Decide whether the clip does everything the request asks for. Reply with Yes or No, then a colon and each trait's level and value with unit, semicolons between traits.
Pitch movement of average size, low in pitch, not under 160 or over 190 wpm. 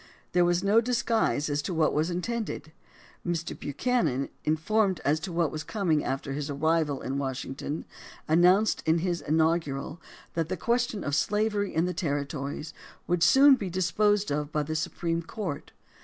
No: average, 4.9 semitones; medium, 165 Hz; average, 170 wpm